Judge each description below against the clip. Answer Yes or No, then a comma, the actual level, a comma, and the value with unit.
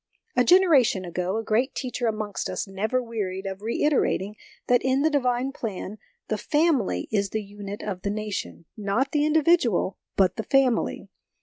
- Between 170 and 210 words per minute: Yes, average, 175 wpm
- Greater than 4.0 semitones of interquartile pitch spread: Yes, average, 4.8 semitones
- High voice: Yes, high, 220 Hz